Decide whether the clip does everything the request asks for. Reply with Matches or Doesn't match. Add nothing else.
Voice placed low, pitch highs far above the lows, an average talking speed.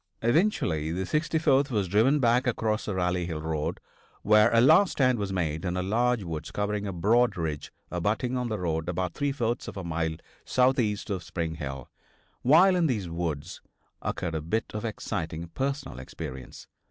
Matches